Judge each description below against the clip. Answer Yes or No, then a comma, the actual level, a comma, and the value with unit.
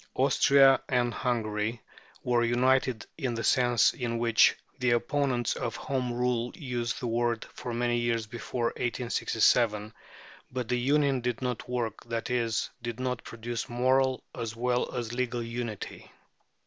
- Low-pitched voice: Yes, low, 120 Hz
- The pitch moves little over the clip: Yes, narrow, 1.3 semitones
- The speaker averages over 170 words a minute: No, average, 145 wpm